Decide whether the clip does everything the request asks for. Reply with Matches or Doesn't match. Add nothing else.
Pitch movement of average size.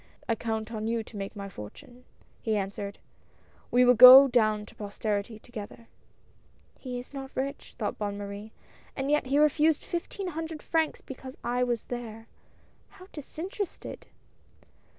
Matches